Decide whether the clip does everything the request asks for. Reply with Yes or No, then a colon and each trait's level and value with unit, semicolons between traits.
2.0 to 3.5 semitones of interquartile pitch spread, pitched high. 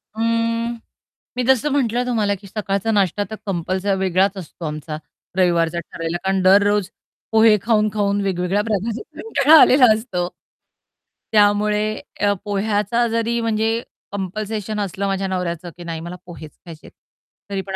Yes: average, 3.2 semitones; high, 205 Hz